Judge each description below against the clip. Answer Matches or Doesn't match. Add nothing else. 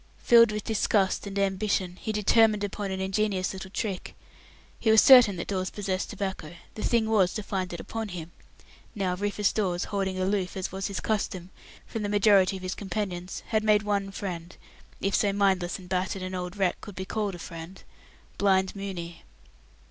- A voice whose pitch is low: Doesn't match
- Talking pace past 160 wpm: Matches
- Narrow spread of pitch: Matches